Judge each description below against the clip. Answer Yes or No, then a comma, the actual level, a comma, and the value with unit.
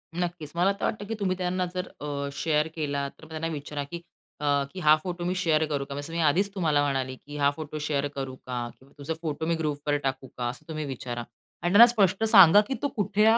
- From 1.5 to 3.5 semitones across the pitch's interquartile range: No, average, 4.3 semitones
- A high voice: No, medium, 155 Hz